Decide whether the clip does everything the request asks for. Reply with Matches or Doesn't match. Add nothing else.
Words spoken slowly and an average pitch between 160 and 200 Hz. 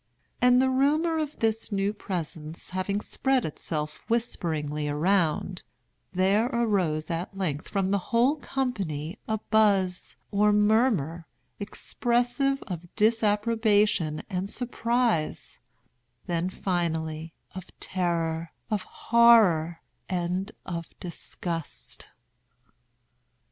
Matches